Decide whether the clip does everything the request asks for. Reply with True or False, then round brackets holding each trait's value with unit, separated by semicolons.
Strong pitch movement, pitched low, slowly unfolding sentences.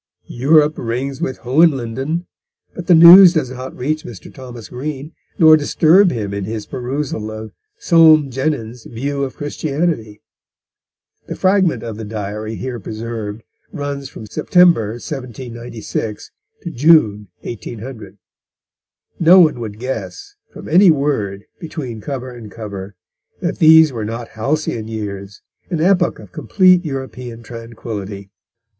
True (5.9 semitones; 125 Hz; 130 wpm)